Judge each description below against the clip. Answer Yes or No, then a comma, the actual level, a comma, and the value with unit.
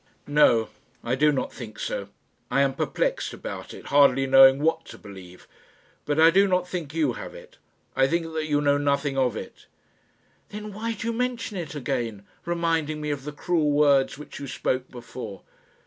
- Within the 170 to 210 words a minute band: Yes, average, 185 wpm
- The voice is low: No, medium, 145 Hz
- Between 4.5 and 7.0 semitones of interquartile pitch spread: No, average, 3.8 semitones